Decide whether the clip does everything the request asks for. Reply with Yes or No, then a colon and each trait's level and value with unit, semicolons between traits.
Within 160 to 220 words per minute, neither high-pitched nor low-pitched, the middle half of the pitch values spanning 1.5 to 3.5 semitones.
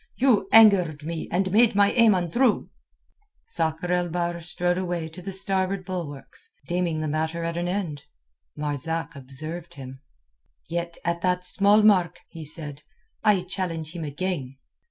No: average, 150 wpm; medium, 175 Hz; average, 2.8 semitones